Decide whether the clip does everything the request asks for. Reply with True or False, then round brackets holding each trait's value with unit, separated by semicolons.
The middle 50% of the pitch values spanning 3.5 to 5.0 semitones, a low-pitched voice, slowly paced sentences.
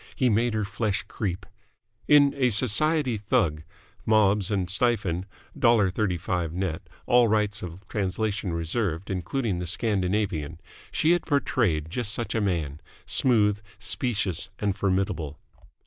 True (4.1 semitones; 100 Hz; 125 wpm)